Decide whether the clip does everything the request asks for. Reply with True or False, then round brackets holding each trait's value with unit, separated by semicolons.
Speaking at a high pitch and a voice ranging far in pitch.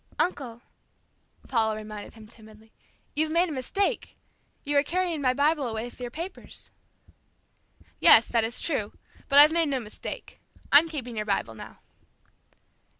True (255 Hz; 5.9 semitones)